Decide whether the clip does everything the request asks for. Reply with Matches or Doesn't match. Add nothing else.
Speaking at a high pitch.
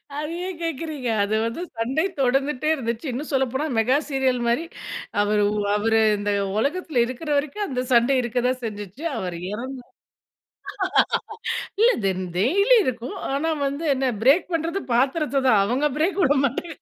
Matches